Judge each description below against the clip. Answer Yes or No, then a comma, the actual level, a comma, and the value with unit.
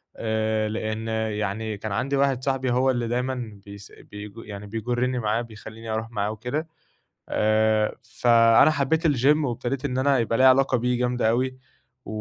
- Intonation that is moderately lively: Yes, average, 3.1 semitones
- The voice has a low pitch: Yes, low, 120 Hz